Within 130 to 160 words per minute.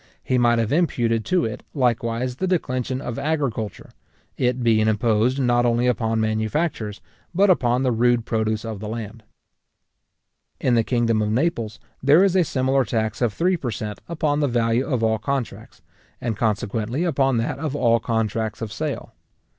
No: average, 170 wpm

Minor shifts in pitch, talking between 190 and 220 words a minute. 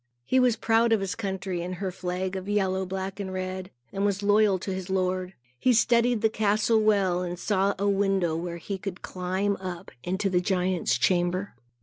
Yes: narrow, 1.9 semitones; average, 195 wpm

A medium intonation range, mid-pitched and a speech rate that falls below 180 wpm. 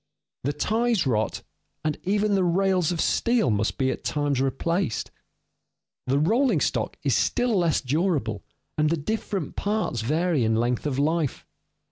No: wide, 6.7 semitones; medium, 160 Hz; average, 150 wpm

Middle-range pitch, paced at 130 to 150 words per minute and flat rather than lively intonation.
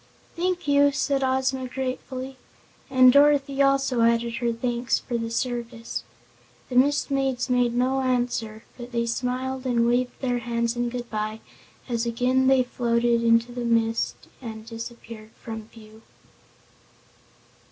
No: high, 245 Hz; average, 140 wpm; narrow, 2.0 semitones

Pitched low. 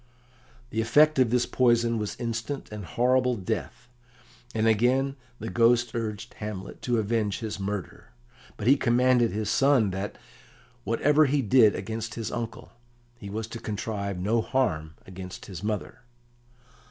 Yes: low, 115 Hz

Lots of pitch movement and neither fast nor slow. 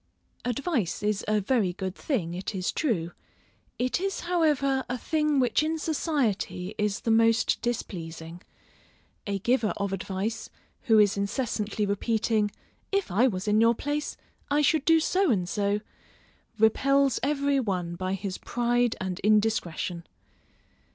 Yes: wide, 5.7 semitones; average, 145 wpm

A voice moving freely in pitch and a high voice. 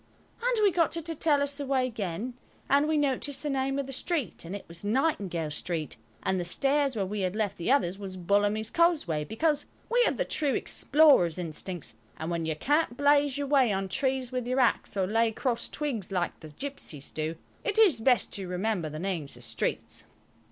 Yes: wide, 7.8 semitones; high, 230 Hz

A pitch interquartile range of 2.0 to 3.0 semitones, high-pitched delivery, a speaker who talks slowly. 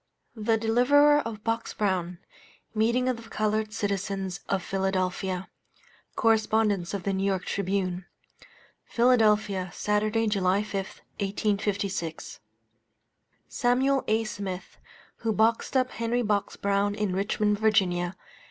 Yes: narrow, 2.6 semitones; high, 210 Hz; slow, 110 wpm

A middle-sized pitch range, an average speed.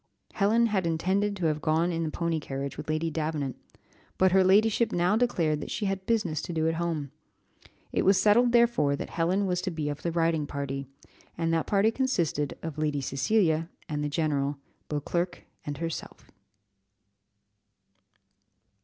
Yes: average, 4.2 semitones; average, 165 wpm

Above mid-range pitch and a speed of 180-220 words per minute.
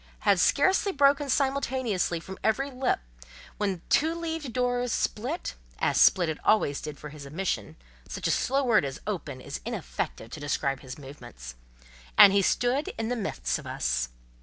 No: high, 200 Hz; average, 165 wpm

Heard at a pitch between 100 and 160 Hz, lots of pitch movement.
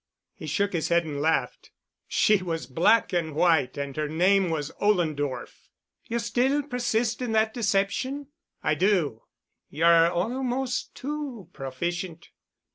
No: medium, 185 Hz; wide, 6.4 semitones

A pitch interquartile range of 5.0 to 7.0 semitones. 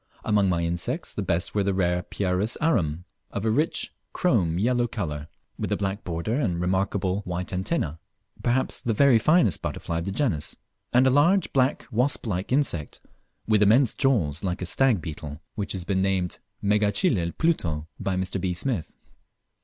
Yes: wide, 5.6 semitones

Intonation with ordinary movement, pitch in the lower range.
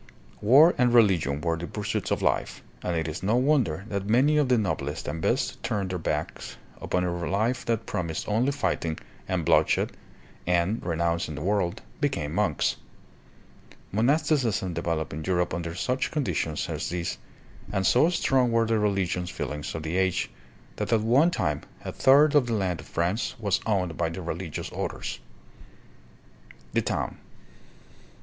No: wide, 6.0 semitones; very low, 95 Hz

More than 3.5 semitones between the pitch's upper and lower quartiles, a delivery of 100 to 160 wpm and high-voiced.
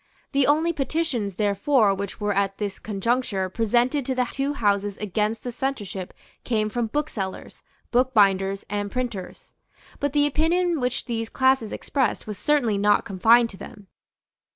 Yes: average, 4.8 semitones; average, 150 wpm; high, 225 Hz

